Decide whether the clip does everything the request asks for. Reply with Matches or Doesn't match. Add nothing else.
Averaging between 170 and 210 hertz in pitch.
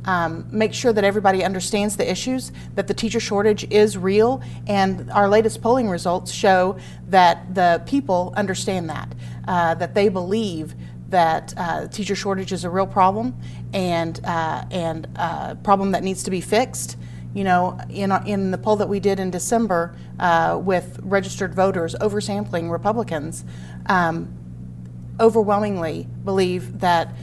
Matches